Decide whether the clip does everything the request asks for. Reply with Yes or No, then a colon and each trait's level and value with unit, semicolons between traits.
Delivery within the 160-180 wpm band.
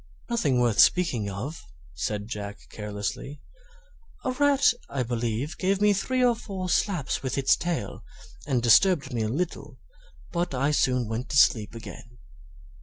No: average, 150 wpm